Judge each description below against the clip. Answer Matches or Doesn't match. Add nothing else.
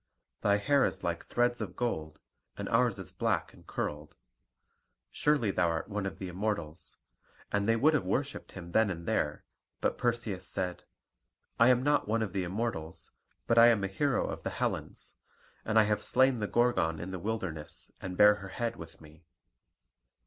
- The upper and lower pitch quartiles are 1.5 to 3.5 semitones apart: Doesn't match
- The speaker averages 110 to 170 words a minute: Doesn't match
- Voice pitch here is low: Matches